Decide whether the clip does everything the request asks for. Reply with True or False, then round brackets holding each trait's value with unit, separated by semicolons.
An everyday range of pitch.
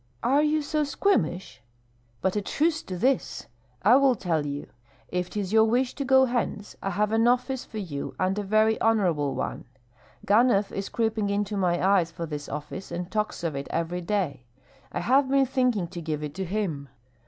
False (6.0 semitones)